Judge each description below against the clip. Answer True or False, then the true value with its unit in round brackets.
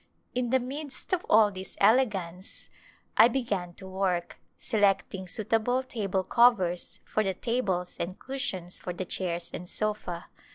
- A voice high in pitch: True (200 Hz)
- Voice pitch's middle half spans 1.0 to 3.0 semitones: False (4.9 semitones)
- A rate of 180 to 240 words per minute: False (140 wpm)